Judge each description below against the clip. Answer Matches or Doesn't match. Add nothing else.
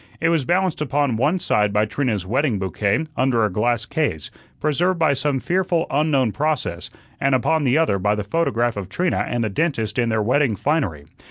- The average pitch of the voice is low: Matches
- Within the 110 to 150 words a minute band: Doesn't match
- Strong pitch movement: Matches